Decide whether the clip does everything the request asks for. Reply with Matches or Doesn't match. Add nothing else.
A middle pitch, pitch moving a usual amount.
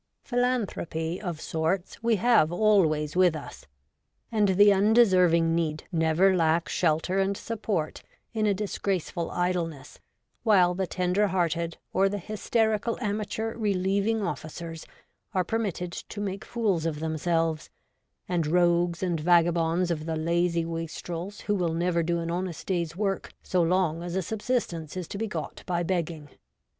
Matches